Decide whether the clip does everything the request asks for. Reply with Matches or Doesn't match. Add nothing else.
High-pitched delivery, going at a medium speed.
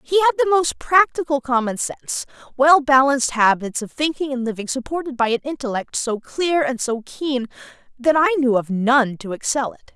Matches